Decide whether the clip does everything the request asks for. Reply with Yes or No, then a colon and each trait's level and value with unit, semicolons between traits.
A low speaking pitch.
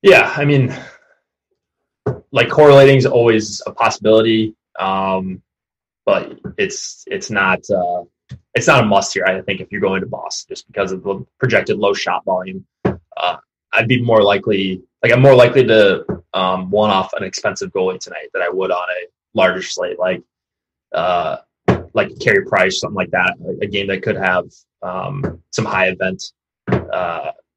Yes: low, 110 Hz